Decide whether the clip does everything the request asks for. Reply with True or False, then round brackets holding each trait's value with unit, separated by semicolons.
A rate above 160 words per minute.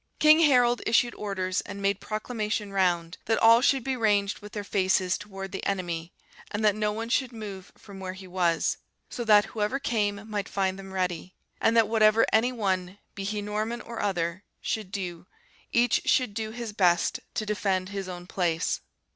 True (185 wpm)